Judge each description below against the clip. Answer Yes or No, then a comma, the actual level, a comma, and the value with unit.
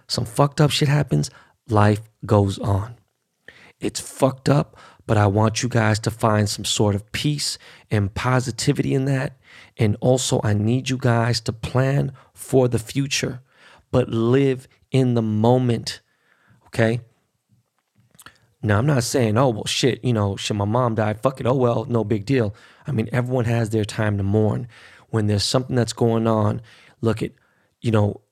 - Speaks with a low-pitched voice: Yes, low, 115 Hz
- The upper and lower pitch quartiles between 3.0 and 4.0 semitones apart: Yes, average, 3.4 semitones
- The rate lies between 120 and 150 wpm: No, average, 170 wpm